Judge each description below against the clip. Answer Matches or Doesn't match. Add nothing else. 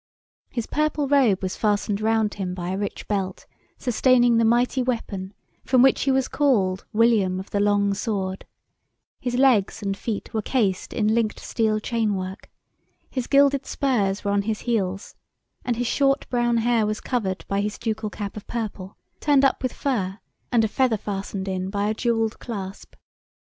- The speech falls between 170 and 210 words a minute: Matches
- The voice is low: Doesn't match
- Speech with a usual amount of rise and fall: Matches